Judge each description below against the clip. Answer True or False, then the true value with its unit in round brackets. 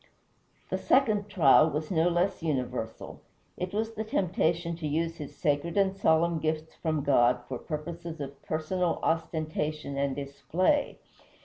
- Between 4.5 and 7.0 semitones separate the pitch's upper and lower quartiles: False (3.2 semitones)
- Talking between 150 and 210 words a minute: False (140 wpm)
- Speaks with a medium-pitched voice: True (160 Hz)